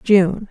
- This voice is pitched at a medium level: No, high, 195 Hz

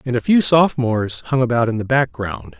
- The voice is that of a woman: No, male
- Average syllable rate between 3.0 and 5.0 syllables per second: No, 5.6 syllables/s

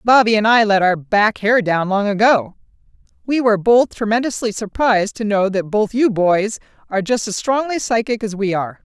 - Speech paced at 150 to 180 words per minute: No, average, 190 wpm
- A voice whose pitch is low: No, high, 215 Hz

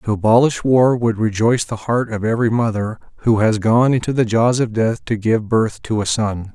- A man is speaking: Yes, male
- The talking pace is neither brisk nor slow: No, fast, 220 wpm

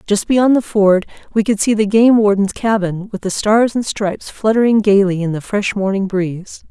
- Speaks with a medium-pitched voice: No, high, 205 Hz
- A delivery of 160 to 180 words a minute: No, fast, 205 wpm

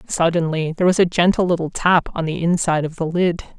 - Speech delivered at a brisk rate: Yes, fast, 215 wpm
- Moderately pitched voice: Yes, medium, 170 Hz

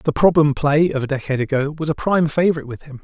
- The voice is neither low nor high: Yes, medium, 150 Hz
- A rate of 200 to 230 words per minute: No, fast, 255 wpm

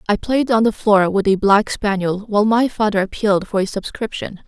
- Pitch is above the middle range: Yes, high, 210 Hz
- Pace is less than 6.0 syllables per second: Yes, 5.4 syllables/s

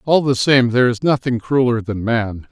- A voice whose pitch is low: Yes, low, 125 Hz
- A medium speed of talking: No, fast, 215 wpm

